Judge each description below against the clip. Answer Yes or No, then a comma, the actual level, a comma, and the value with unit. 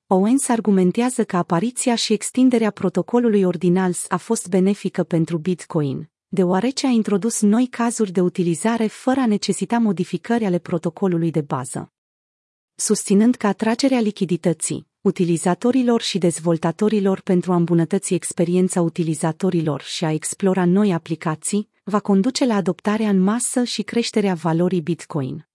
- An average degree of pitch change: Yes, average, 4.0 semitones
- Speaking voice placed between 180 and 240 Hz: Yes, high, 190 Hz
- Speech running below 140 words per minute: Yes, average, 130 wpm